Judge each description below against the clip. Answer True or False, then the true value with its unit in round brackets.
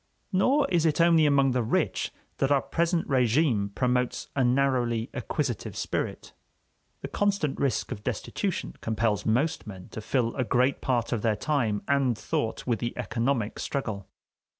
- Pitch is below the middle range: True (125 Hz)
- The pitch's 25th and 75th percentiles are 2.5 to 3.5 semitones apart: False (3.9 semitones)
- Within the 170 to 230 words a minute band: False (155 wpm)